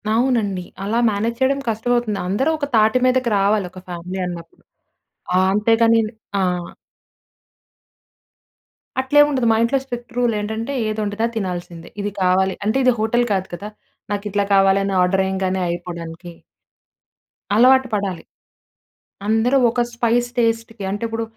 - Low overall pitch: No, high, 215 Hz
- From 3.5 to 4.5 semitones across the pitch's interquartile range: Yes, average, 3.8 semitones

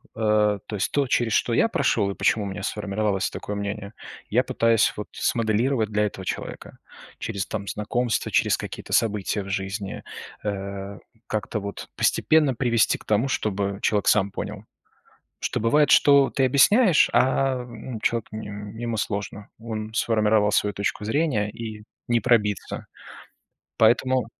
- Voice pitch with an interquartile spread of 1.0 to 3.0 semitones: Yes, narrow, 2.5 semitones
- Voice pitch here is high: No, low, 110 Hz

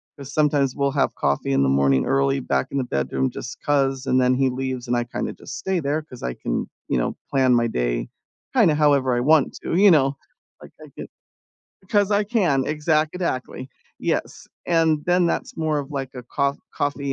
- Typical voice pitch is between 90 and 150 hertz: Yes, medium, 140 Hz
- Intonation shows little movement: No, average, 3.8 semitones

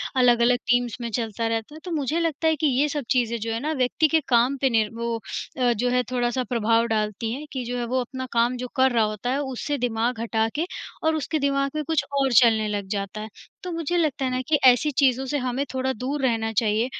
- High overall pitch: Yes, very high, 250 Hz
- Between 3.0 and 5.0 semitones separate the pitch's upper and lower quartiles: Yes, average, 3.3 semitones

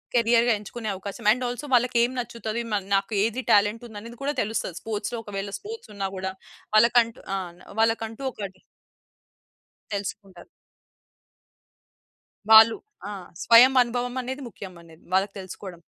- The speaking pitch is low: No, high, 225 Hz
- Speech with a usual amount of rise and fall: Yes, average, 3.2 semitones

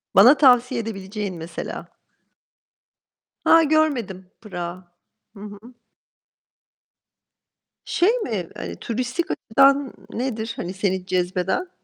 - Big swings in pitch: Yes, wide, 6.0 semitones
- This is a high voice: Yes, high, 220 Hz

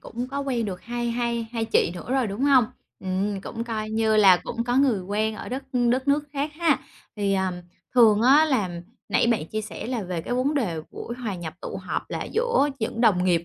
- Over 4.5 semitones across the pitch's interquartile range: No, average, 4.2 semitones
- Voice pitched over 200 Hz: Yes, high, 230 Hz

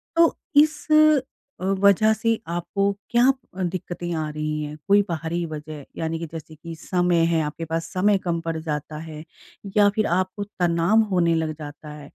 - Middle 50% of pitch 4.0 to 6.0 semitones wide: No, average, 3.3 semitones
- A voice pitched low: No, medium, 170 Hz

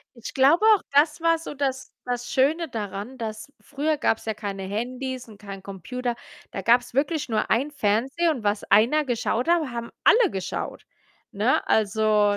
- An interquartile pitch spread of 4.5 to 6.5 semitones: Yes, average, 5.0 semitones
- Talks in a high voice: Yes, high, 245 Hz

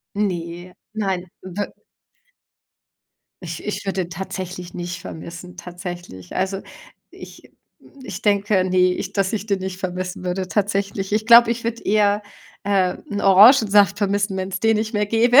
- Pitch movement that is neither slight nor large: No, narrow, 2.3 semitones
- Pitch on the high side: Yes, high, 195 Hz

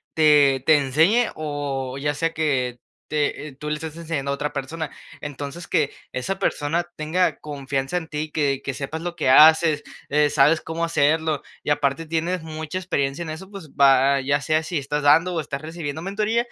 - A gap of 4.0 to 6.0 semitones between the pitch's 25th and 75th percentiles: No, narrow, 2.6 semitones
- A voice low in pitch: No, medium, 150 Hz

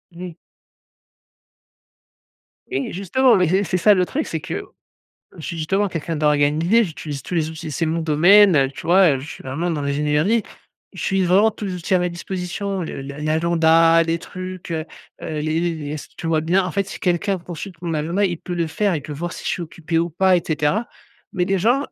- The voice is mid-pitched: Yes, medium, 170 Hz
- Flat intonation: No, average, 3.1 semitones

